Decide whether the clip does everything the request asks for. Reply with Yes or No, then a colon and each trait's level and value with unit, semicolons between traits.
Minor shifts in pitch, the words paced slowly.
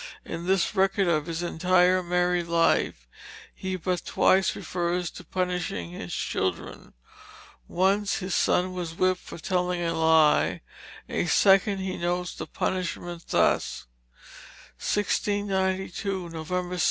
Yes: narrow, 1.9 semitones; slow, 130 wpm